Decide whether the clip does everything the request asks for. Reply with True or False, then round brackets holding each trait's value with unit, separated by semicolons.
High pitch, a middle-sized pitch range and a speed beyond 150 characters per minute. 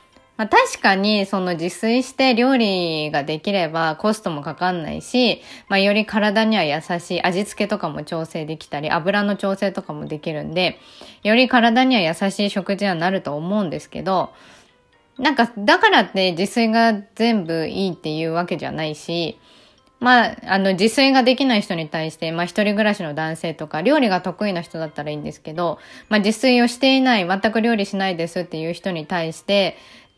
True (195 Hz; 4.9 semitones; 365 characters per minute)